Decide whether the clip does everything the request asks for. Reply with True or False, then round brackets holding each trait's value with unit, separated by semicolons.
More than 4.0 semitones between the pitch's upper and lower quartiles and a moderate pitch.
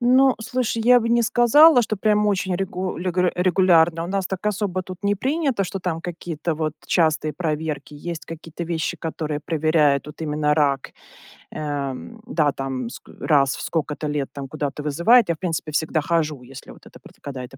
True (4.5 semitones; 165 Hz)